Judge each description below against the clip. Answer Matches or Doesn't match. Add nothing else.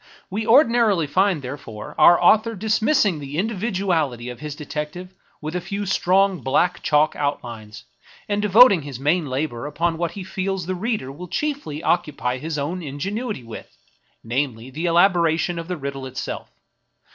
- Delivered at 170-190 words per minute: Doesn't match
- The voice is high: Doesn't match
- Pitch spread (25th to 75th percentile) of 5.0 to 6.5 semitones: Matches